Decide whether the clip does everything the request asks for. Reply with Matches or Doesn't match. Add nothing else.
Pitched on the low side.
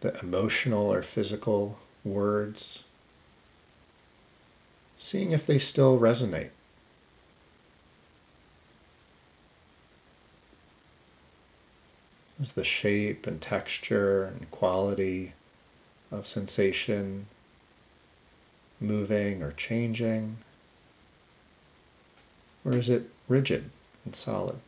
Matches